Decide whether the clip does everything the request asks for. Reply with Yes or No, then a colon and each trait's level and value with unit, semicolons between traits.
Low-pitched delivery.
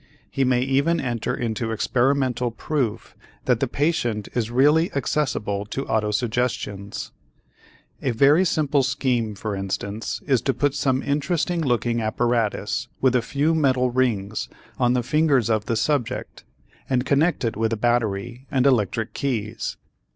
Yes: low, 125 Hz